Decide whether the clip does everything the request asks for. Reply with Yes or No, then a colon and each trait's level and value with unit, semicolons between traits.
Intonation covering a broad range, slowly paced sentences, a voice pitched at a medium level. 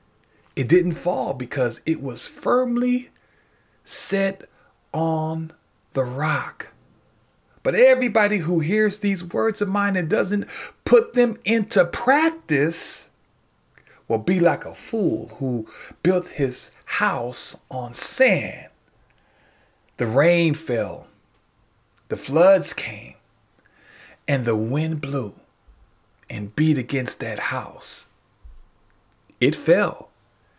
Yes: wide, 9.0 semitones; slow, 105 wpm; medium, 160 Hz